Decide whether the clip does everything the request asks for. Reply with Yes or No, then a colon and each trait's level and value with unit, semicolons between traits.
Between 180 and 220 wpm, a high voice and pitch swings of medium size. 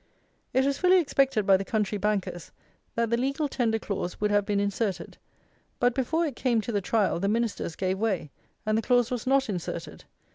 Yes: average, 195 wpm; high, 220 Hz; average, 4.1 semitones